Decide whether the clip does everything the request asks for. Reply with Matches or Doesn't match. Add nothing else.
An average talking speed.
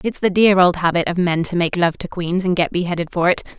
Doesn't match